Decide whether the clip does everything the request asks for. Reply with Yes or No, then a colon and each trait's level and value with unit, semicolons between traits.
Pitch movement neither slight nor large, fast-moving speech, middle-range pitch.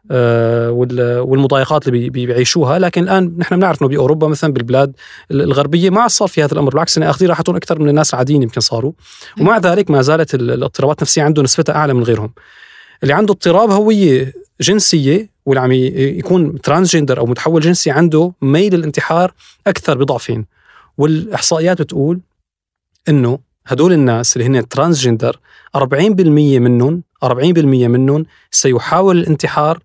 Yes: average, 4.6 semitones; fast, 140 wpm; medium, 150 Hz